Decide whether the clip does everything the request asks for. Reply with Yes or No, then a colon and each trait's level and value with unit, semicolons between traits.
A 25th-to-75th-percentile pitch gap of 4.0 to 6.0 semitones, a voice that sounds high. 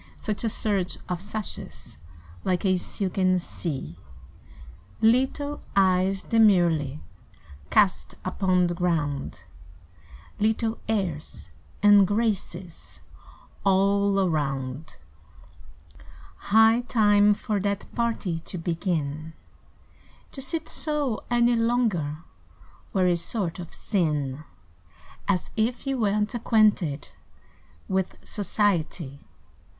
Yes: average, 4.4 semitones; high, 195 Hz